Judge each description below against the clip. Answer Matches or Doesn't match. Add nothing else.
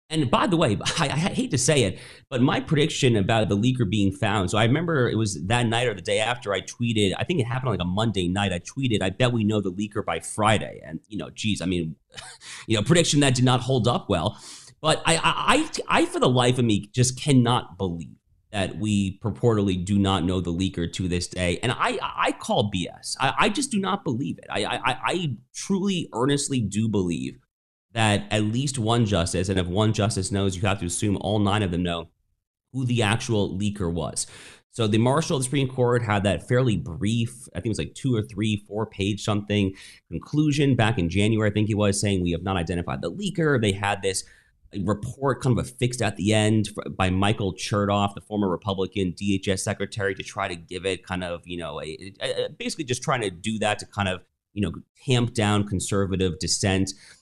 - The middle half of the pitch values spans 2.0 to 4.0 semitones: Doesn't match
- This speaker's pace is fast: Matches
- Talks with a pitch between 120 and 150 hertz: Doesn't match